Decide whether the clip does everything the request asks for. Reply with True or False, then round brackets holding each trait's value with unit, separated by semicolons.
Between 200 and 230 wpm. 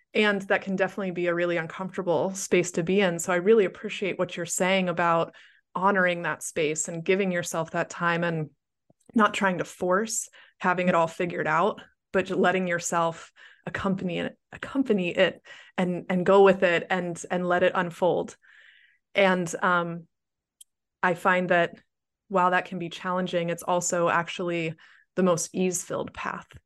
False (165 wpm)